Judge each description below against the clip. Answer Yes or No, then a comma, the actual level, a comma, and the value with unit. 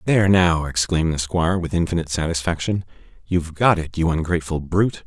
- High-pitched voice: No, very low, 85 Hz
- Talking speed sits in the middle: Yes, average, 165 wpm